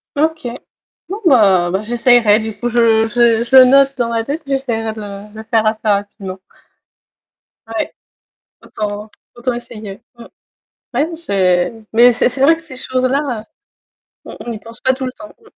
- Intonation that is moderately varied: Yes, average, 3.4 semitones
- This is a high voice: Yes, high, 235 Hz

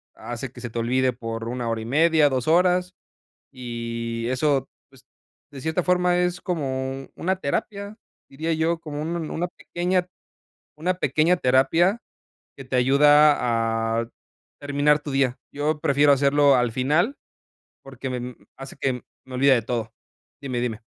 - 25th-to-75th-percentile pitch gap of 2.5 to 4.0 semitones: No, average, 4.4 semitones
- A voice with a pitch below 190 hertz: Yes, low, 135 Hz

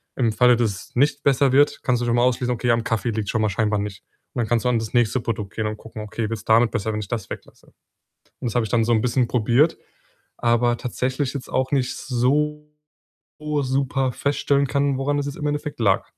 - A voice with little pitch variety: No, average, 3.3 semitones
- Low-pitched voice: Yes, low, 120 Hz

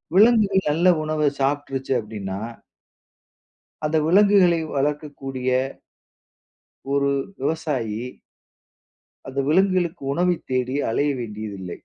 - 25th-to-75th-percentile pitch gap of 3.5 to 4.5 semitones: No, average, 5.2 semitones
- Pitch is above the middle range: No, medium, 145 Hz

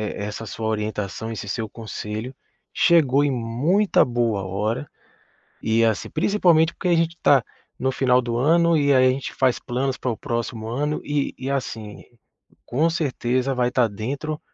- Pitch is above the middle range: No, low, 125 Hz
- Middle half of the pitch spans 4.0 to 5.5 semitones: Yes, average, 4.5 semitones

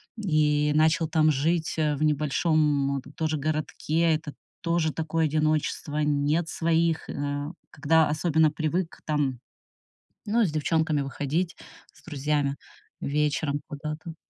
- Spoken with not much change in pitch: Yes, narrow, 1.8 semitones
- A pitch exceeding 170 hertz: No, medium, 155 Hz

